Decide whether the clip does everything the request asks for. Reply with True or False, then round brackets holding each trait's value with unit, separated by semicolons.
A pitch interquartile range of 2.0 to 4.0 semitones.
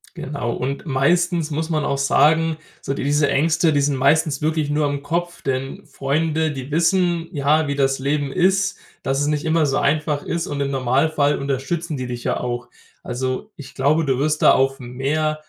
True (2.7 semitones)